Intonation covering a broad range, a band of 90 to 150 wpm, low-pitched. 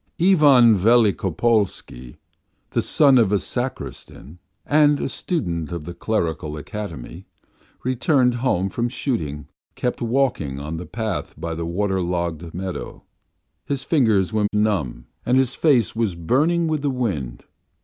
Yes: wide, 7.2 semitones; average, 140 wpm; low, 105 Hz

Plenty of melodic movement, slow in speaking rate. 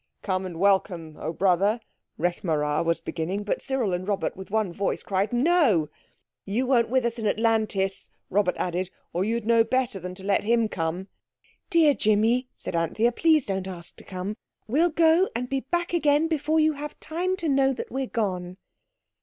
No: wide, 6.4 semitones; average, 185 wpm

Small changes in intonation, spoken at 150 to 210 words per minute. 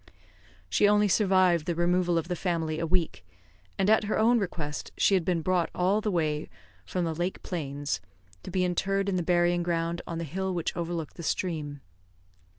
Yes: narrow, 2.3 semitones; average, 185 wpm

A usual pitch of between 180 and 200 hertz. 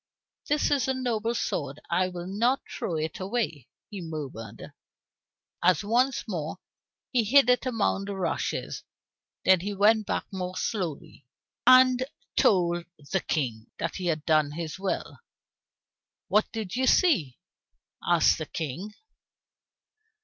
Yes: high, 190 Hz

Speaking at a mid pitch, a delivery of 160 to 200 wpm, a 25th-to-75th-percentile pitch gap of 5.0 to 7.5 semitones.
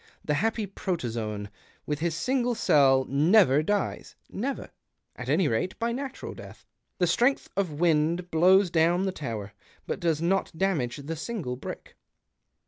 No: medium, 170 Hz; average, 150 wpm; average, 5.3 semitones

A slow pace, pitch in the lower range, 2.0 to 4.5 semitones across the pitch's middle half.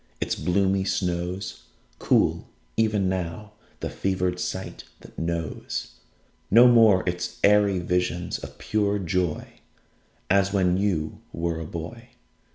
Yes: slow, 120 wpm; very low, 95 Hz; narrow, 2.6 semitones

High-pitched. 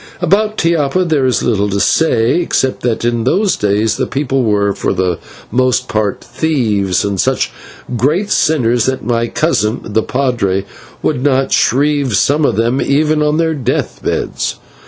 No: low, 130 Hz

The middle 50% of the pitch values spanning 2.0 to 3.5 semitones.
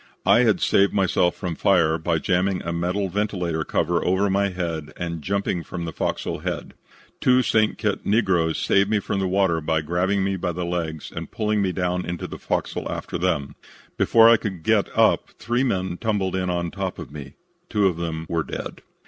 Yes: average, 2.8 semitones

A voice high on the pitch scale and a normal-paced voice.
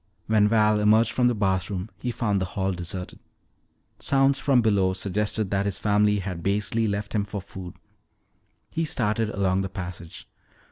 No: low, 105 Hz; average, 160 wpm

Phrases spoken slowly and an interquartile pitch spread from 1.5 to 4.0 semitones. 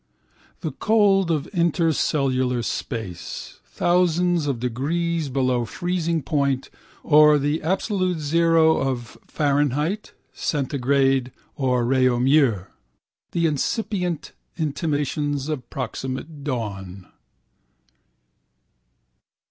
No: slow, 80 wpm; average, 4.4 semitones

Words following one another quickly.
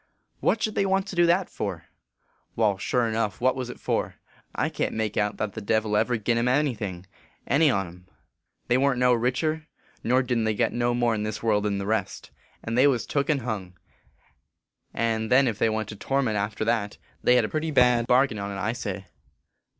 Yes: fast, 230 wpm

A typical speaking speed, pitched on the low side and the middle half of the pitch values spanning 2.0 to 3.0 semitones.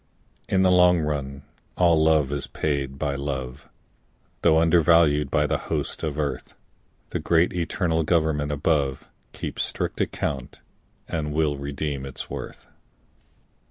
No: slow, 130 wpm; very low, 75 Hz; average, 2.7 semitones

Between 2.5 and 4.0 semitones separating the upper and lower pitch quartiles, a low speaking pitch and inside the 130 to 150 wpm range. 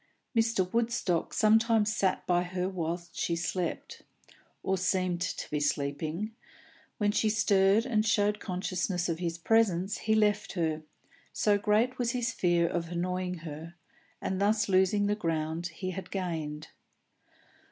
No: average, 3.7 semitones; medium, 185 Hz; average, 140 wpm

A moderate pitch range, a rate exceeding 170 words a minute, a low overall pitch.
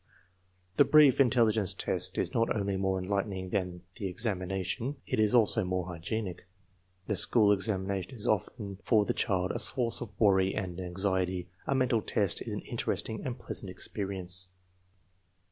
No: average, 3.1 semitones; average, 155 wpm; low, 100 Hz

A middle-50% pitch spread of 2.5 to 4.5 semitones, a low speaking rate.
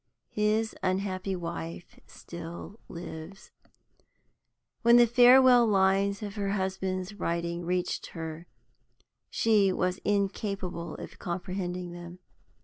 Yes: average, 2.9 semitones; slow, 100 wpm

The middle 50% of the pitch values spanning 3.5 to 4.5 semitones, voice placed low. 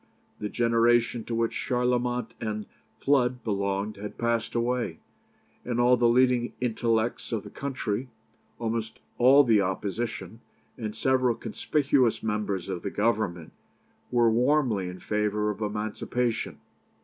No: average, 2.7 semitones; low, 115 Hz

